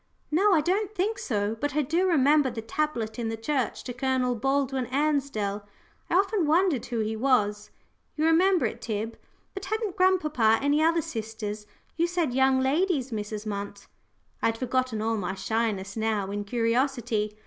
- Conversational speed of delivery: Yes, average, 170 wpm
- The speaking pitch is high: Yes, very high, 255 Hz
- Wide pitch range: Yes, wide, 5.8 semitones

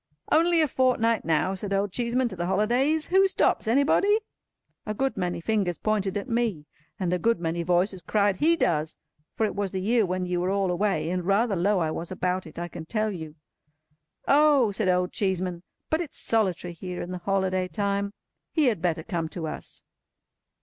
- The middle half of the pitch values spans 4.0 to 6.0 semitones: Yes, average, 4.4 semitones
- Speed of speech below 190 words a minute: No, average, 195 wpm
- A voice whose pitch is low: No, high, 195 Hz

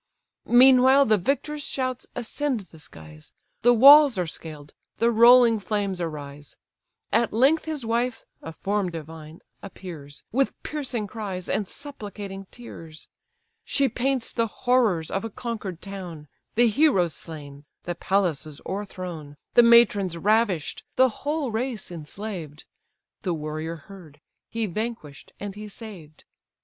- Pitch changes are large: Yes, wide, 6.7 semitones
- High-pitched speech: Yes, high, 205 Hz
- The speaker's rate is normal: No, slow, 130 wpm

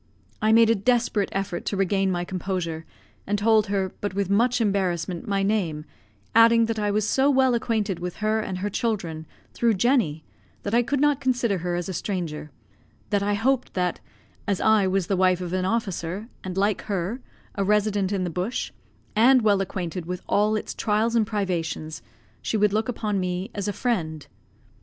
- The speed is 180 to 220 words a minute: Yes, average, 190 wpm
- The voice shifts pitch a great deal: No, average, 3.4 semitones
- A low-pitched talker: No, high, 200 Hz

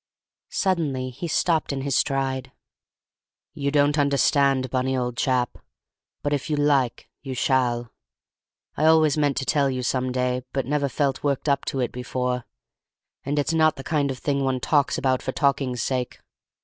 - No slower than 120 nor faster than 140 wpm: No, average, 170 wpm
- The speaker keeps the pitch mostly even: Yes, narrow, 2.1 semitones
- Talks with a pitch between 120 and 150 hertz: Yes, low, 135 Hz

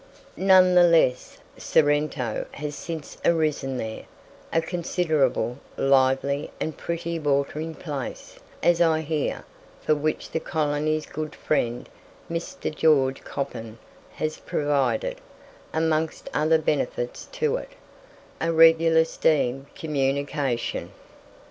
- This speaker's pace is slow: Yes, slow, 105 wpm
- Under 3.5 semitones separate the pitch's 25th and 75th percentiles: Yes, average, 2.8 semitones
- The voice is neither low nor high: Yes, medium, 155 Hz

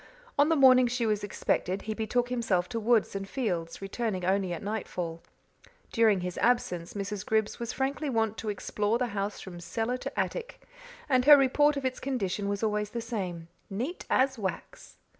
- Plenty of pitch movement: No, average, 4.2 semitones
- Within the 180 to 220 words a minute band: Yes, average, 185 wpm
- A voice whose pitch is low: No, high, 220 Hz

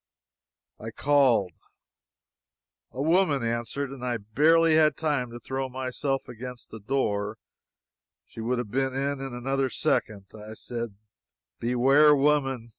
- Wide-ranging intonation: No, average, 3.1 semitones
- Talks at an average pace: No, slow, 130 wpm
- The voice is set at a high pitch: No, low, 130 Hz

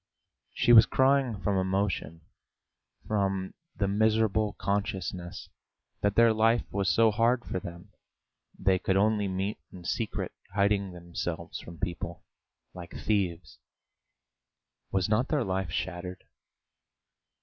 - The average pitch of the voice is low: Yes, low, 100 Hz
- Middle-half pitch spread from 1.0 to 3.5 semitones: Yes, average, 3.0 semitones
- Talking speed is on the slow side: Yes, slow, 115 wpm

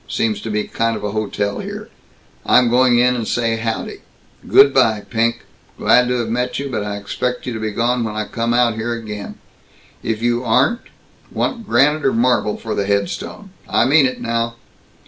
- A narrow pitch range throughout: Yes, narrow, 2.3 semitones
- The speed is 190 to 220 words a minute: Yes, average, 195 wpm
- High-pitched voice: No, low, 115 Hz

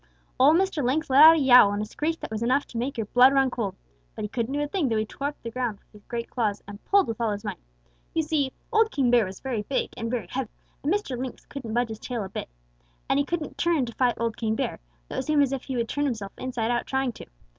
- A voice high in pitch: Yes, very high, 250 Hz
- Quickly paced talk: Yes, fast, 285 wpm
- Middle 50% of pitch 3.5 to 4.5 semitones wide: Yes, average, 4.0 semitones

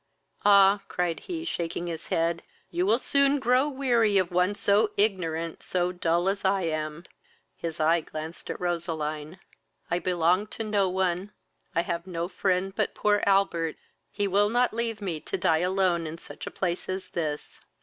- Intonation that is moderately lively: Yes, average, 3.4 semitones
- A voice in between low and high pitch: Yes, medium, 180 Hz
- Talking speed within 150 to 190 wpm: Yes, average, 170 wpm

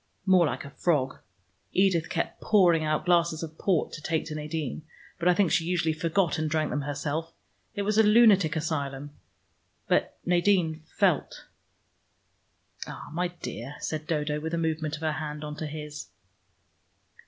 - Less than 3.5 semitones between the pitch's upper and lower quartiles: Yes, narrow, 2.5 semitones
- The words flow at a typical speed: Yes, average, 165 wpm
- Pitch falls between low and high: Yes, medium, 160 Hz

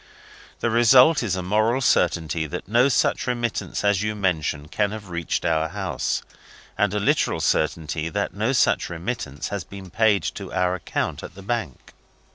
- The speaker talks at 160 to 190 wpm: Yes, average, 170 wpm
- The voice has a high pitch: No, low, 100 Hz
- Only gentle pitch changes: No, average, 4.6 semitones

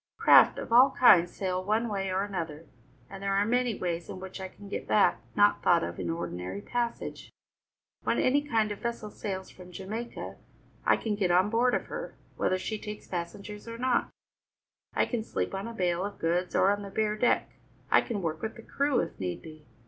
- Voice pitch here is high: Yes, high, 200 Hz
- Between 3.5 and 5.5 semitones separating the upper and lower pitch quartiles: Yes, average, 4.2 semitones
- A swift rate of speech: Yes, fast, 210 wpm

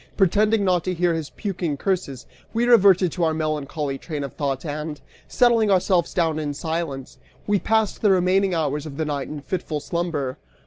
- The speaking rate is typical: Yes, average, 180 wpm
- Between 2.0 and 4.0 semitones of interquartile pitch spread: No, average, 4.4 semitones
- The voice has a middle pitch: Yes, medium, 165 Hz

